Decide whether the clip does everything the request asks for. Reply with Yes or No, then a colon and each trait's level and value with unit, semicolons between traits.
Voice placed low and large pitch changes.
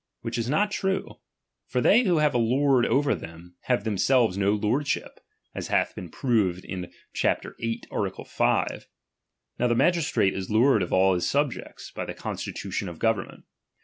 Yes: low, 115 Hz; wide, 6.4 semitones